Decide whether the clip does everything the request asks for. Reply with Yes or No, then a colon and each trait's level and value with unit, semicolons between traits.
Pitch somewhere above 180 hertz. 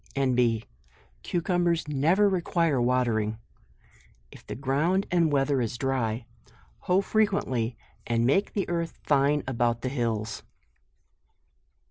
No: low, 135 Hz